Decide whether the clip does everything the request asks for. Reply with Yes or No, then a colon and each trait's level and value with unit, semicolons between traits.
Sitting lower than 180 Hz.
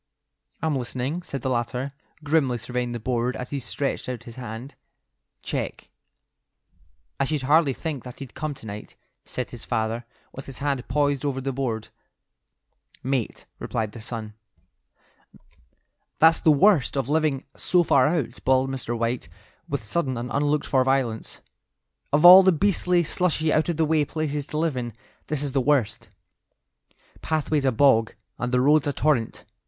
Yes: low, 135 Hz